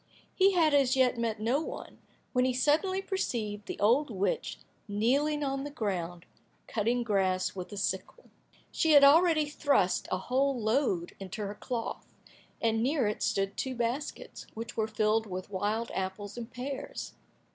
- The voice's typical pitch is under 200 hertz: No, high, 235 Hz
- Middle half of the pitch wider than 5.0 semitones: Yes, wide, 5.4 semitones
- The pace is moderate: Yes, average, 160 wpm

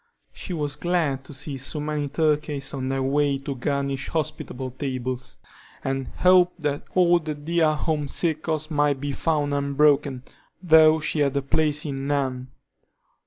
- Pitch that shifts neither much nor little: No, narrow, 2.3 semitones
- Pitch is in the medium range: Yes, medium, 145 Hz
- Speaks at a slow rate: No, average, 150 wpm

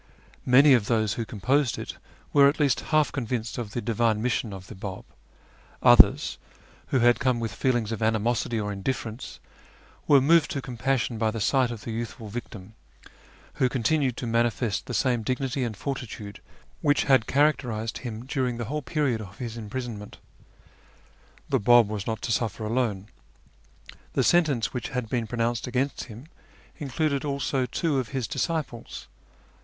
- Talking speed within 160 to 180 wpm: Yes, average, 165 wpm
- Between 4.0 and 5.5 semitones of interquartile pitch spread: No, average, 3.2 semitones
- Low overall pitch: Yes, low, 120 Hz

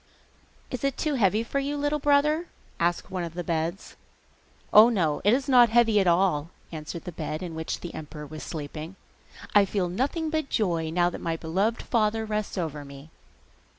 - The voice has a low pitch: No, high, 190 Hz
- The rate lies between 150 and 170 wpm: No, average, 185 wpm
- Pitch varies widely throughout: Yes, wide, 6.7 semitones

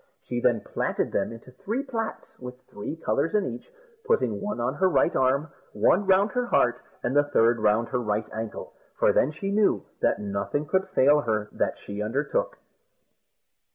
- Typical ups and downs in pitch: No, wide, 8.7 semitones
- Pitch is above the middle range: No, low, 135 Hz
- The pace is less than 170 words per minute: No, average, 185 wpm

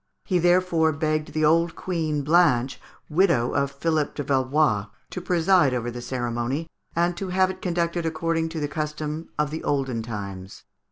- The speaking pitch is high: No, medium, 155 Hz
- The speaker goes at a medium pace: Yes, average, 160 wpm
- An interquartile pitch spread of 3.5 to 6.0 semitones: Yes, average, 4.1 semitones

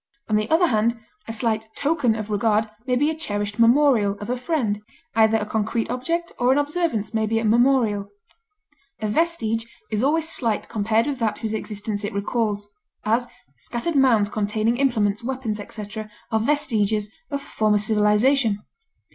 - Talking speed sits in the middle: Yes, average, 165 wpm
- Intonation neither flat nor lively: Yes, average, 3.5 semitones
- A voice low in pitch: No, high, 225 Hz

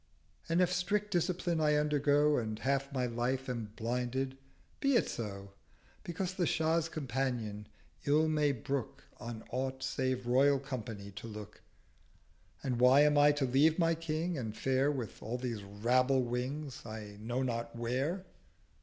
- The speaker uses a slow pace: No, average, 145 wpm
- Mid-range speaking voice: No, low, 130 Hz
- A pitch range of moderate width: Yes, average, 4.1 semitones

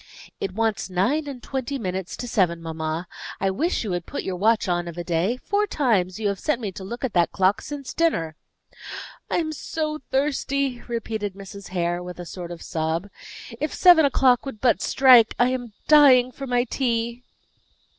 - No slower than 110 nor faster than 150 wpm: No, average, 190 wpm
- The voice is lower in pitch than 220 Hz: No, high, 225 Hz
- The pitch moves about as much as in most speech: No, wide, 6.6 semitones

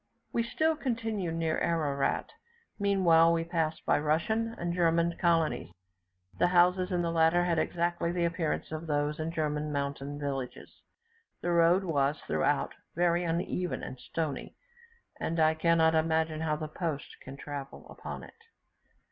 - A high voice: No, medium, 165 Hz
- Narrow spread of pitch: Yes, narrow, 2.2 semitones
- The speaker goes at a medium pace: Yes, average, 145 wpm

